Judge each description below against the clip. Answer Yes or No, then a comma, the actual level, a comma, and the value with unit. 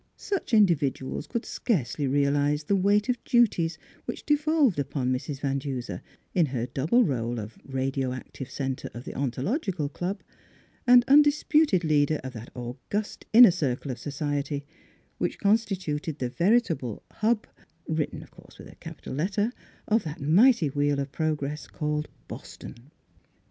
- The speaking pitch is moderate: Yes, medium, 150 Hz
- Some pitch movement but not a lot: No, wide, 7.3 semitones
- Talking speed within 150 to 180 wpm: Yes, average, 155 wpm